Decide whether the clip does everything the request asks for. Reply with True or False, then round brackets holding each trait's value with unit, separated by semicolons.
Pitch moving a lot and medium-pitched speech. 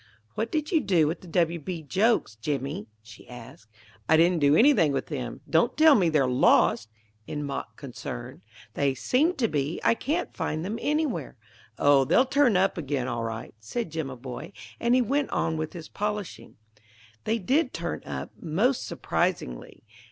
True (8.8 semitones; 165 Hz)